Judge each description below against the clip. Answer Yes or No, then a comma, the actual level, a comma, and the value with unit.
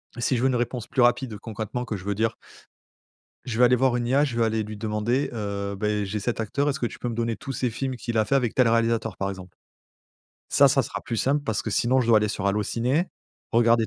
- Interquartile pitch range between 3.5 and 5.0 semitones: No, average, 2.7 semitones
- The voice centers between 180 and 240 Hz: No, low, 115 Hz